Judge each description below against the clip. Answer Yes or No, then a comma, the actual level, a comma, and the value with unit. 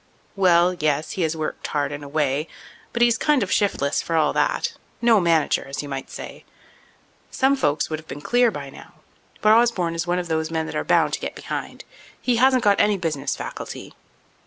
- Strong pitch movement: Yes, wide, 6.0 semitones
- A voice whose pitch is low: No, medium, 170 Hz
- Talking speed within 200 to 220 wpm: Yes, fast, 205 wpm